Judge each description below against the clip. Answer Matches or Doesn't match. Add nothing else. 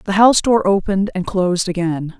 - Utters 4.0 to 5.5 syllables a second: Doesn't match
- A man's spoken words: Doesn't match